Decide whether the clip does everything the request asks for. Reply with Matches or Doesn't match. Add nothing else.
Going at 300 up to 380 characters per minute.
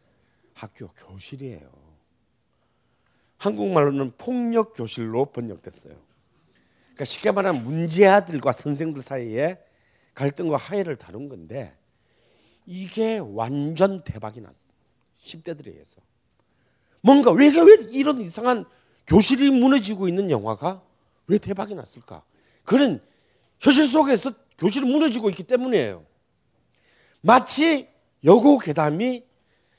Doesn't match